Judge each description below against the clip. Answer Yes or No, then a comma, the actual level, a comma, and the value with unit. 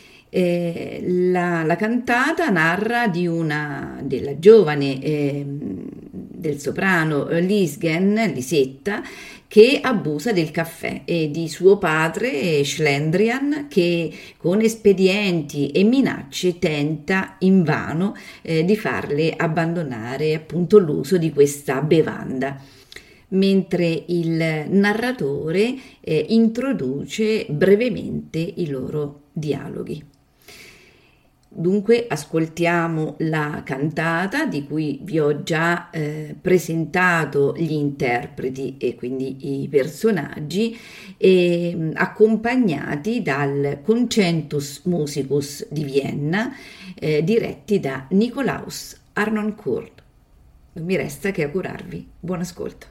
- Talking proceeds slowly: Yes, slow, 95 wpm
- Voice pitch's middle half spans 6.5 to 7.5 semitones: No, wide, 5.4 semitones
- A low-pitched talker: No, medium, 170 Hz